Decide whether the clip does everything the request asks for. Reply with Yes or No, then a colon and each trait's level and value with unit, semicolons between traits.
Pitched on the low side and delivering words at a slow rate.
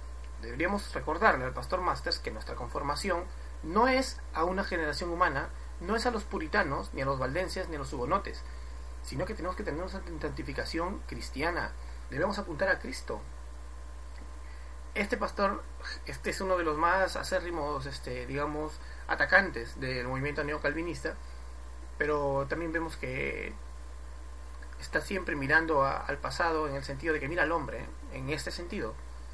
No: low, 110 Hz; average, 155 wpm